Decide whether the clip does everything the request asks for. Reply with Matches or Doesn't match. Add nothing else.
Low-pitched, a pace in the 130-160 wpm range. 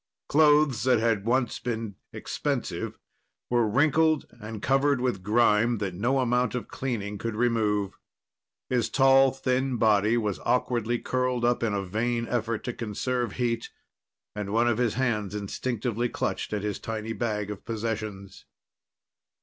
Matches